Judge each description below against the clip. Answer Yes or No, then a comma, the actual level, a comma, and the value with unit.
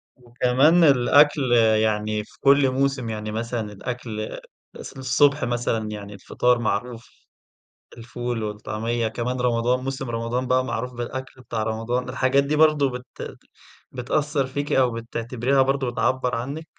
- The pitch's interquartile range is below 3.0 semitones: Yes, narrow, 2.5 semitones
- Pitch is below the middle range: Yes, low, 125 Hz